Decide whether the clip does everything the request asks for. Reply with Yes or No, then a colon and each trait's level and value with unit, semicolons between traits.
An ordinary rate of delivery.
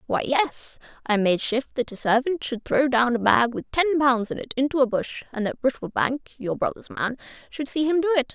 No: fast, 215 wpm